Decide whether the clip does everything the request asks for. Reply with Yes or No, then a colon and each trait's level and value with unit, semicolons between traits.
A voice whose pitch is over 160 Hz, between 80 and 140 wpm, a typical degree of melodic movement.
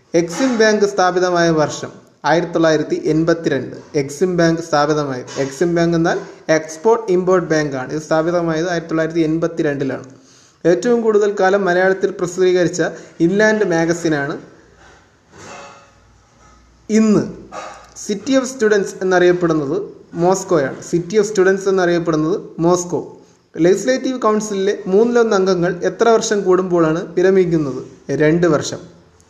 Yes: medium, 175 Hz; average, 100 wpm; average, 3.6 semitones